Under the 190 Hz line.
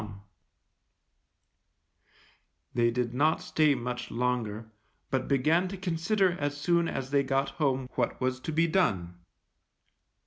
Yes: low, 135 Hz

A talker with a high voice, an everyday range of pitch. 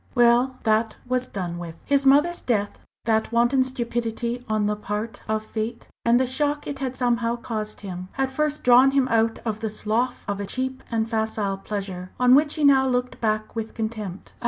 Yes: high, 235 Hz; average, 3.1 semitones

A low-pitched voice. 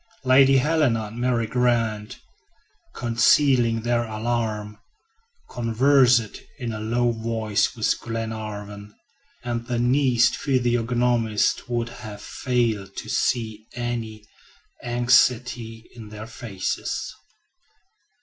Yes: low, 115 Hz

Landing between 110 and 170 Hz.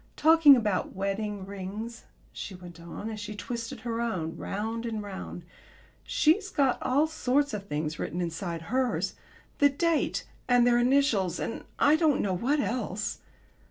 No: high, 225 Hz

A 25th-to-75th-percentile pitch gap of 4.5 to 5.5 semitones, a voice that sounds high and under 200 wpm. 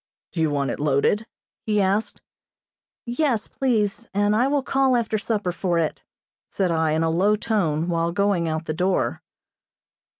Yes: average, 5.1 semitones; high, 195 Hz; average, 165 wpm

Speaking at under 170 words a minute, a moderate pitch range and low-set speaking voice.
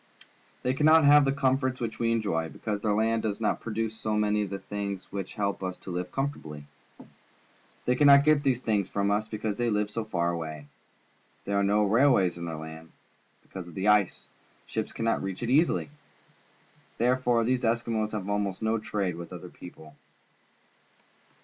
No: average, 180 wpm; average, 3.8 semitones; low, 105 Hz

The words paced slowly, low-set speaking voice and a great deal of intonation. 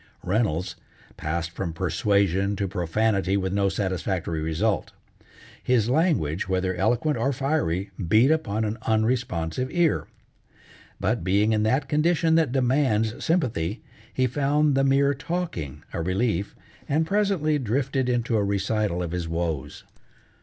Yes: slow, 130 wpm; low, 110 Hz; wide, 6.7 semitones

